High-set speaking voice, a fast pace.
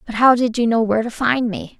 Yes: high, 235 Hz; fast, 300 wpm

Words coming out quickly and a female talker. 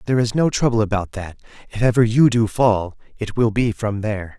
No: fast, 220 wpm; male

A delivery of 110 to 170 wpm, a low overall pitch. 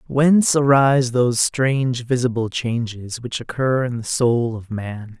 Yes: average, 150 wpm; low, 125 Hz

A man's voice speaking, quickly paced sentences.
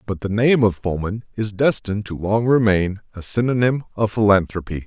No: male; average, 175 wpm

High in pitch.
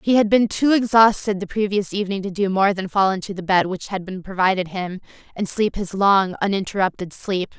Yes: high, 195 Hz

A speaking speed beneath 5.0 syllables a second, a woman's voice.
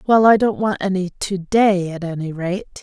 Yes: 4.6 syllables/s; female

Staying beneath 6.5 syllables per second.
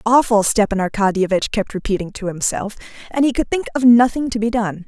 Yes: 5.9 syllables/s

